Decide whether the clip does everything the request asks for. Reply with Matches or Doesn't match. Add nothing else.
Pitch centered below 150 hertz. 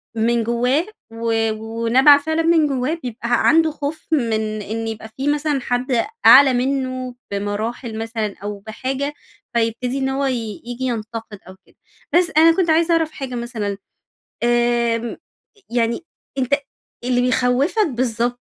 Doesn't match